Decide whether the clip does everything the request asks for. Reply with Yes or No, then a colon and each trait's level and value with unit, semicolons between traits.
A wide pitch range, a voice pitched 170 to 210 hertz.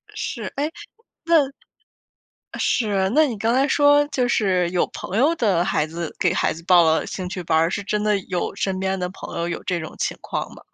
Yes: wide, 5.7 semitones; high, 190 Hz